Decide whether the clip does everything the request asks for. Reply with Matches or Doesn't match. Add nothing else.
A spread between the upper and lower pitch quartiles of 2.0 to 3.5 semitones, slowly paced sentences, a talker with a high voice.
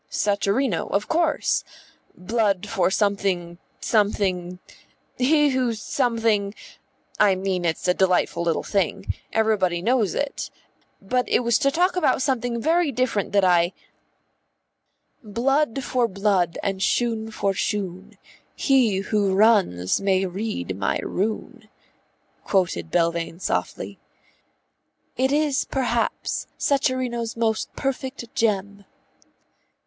Doesn't match